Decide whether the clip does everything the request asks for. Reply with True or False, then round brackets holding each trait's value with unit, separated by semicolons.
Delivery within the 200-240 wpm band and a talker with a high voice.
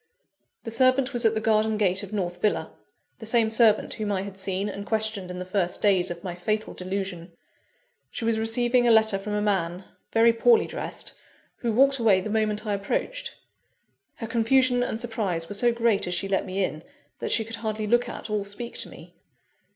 True (205 wpm; 215 Hz)